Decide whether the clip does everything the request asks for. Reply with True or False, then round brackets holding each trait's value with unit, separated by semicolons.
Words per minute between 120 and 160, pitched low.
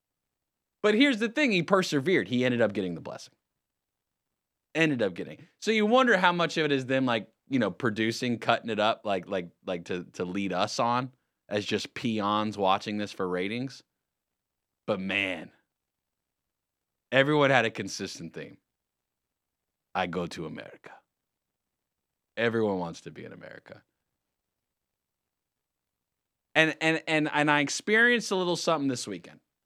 True (150 wpm; 125 Hz)